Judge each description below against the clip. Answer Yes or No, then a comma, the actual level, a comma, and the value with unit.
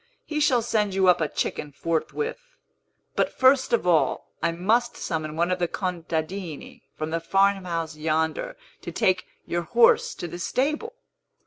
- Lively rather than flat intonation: Yes, wide, 6.1 semitones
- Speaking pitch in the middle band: Yes, medium, 180 Hz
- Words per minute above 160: No, average, 155 wpm